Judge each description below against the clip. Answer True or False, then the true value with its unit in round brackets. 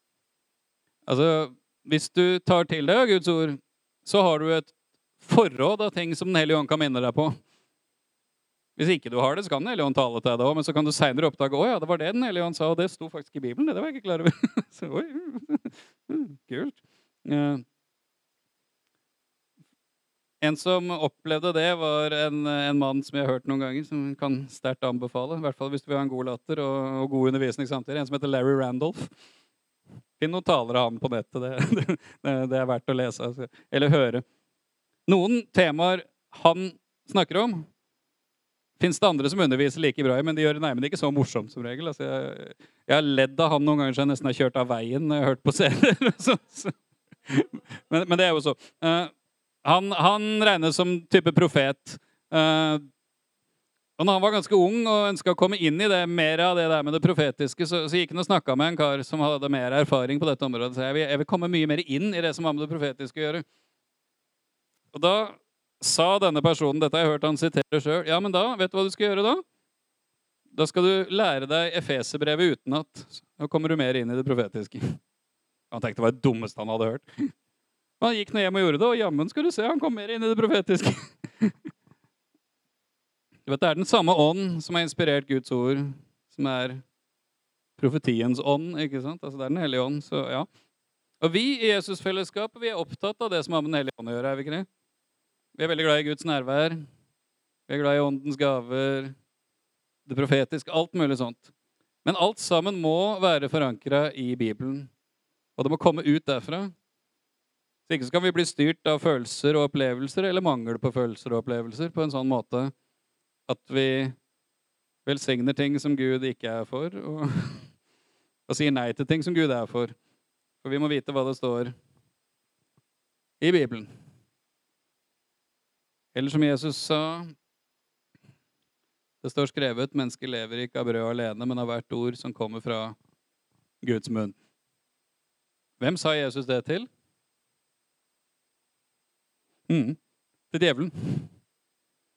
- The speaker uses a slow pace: False (190 wpm)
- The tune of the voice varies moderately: True (4.1 semitones)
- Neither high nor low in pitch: True (150 Hz)